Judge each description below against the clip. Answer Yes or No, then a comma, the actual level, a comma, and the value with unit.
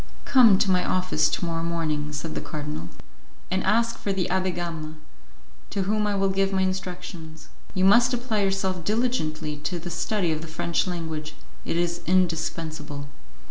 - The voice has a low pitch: No, medium, 175 Hz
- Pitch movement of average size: Yes, average, 3.4 semitones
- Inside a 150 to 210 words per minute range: Yes, average, 170 wpm